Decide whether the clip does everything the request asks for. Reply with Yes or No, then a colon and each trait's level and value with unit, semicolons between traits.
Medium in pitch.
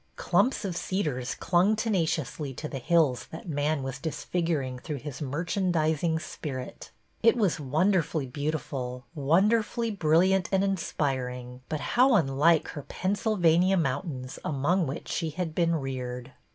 Yes: medium, 160 Hz